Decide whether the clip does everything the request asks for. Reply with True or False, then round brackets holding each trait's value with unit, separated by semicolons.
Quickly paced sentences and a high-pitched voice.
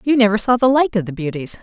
True (295 wpm; 215 Hz)